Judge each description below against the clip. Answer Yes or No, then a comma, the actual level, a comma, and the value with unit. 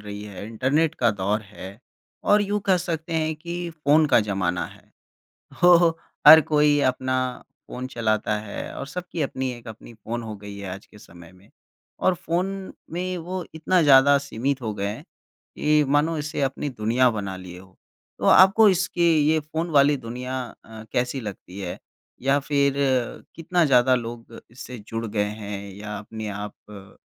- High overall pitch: No, low, 130 Hz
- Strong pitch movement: Yes, wide, 7.1 semitones